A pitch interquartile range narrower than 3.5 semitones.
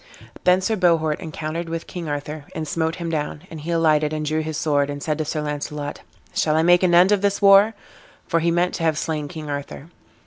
Yes: narrow, 2.4 semitones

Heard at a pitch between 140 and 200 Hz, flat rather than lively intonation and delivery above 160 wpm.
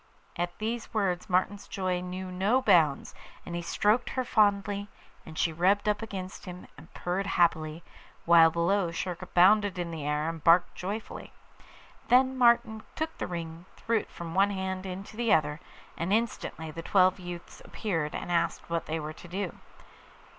No: medium, 185 Hz; average, 3.3 semitones; average, 175 wpm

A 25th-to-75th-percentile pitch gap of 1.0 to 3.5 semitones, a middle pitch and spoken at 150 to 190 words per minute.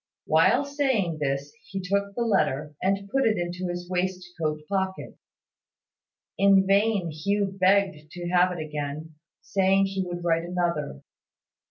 No: average, 3.2 semitones; medium, 180 Hz; average, 140 wpm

